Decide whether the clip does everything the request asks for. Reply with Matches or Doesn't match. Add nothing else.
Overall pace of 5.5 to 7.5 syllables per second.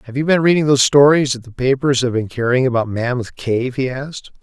Matches